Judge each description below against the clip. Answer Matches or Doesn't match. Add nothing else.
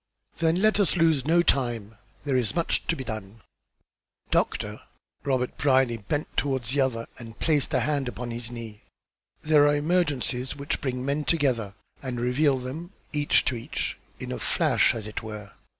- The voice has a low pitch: Matches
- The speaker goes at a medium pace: Matches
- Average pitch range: Matches